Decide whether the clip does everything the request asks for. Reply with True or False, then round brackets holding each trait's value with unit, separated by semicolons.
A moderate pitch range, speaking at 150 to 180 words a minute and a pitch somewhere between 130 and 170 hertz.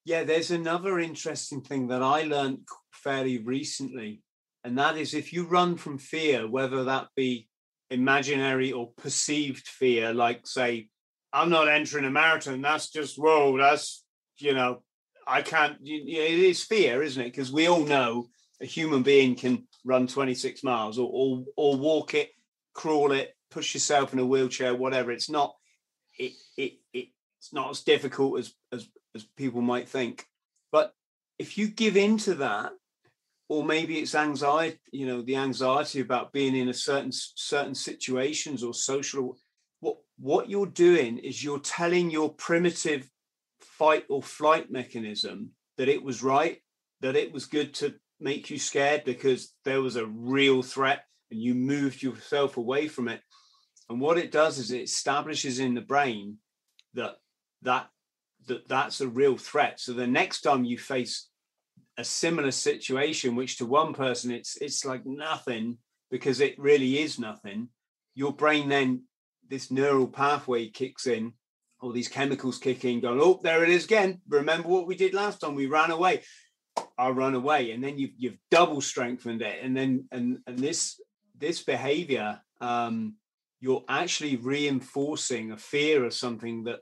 True (3.5 semitones; 165 wpm; 135 Hz)